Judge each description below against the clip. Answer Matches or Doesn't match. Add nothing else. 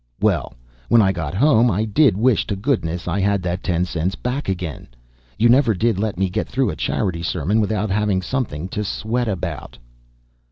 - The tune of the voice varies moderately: Matches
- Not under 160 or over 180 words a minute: Doesn't match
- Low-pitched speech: Matches